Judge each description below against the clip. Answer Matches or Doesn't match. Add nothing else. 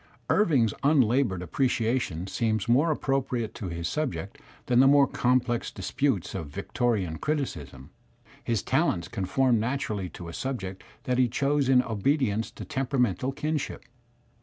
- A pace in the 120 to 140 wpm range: Matches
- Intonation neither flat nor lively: Doesn't match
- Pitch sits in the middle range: Doesn't match